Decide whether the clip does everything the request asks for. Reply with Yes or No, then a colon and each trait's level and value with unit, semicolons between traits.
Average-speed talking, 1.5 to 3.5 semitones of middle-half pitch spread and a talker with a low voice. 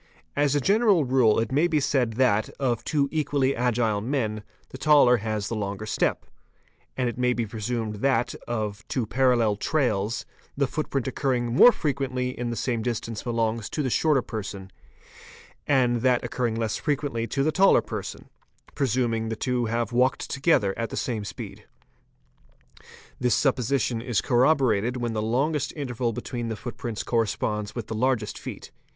Yes: average, 160 wpm; average, 3.2 semitones; low, 120 Hz